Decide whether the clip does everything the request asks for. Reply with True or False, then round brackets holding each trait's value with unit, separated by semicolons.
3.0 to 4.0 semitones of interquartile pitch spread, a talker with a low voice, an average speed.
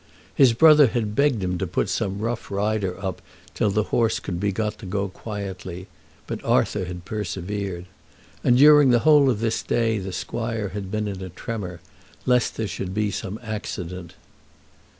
True (3.5 semitones; 105 Hz; 175 wpm)